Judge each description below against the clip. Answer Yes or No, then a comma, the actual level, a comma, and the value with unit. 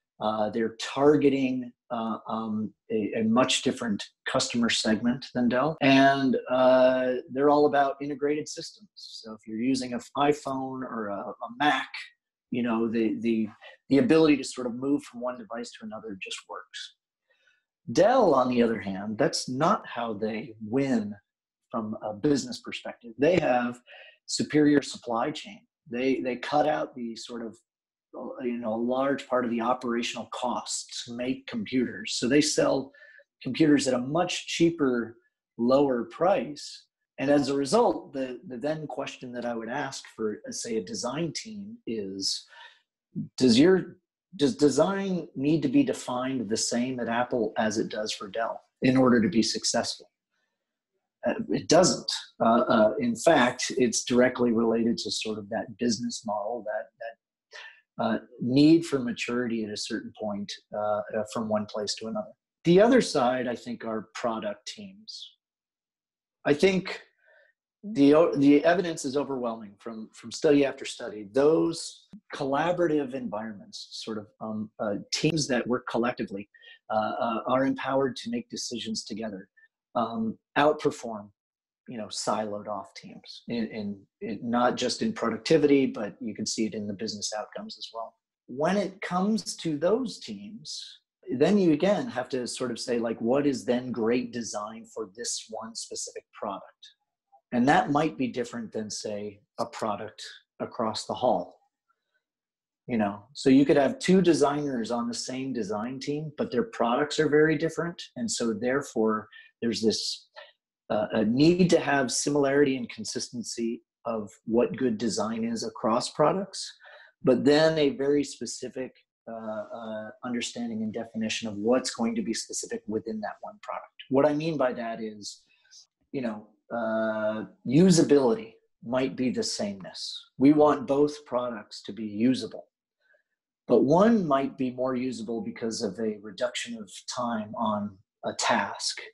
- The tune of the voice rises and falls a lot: Yes, wide, 6.3 semitones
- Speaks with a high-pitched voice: No, low, 130 Hz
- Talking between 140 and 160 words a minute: Yes, average, 155 wpm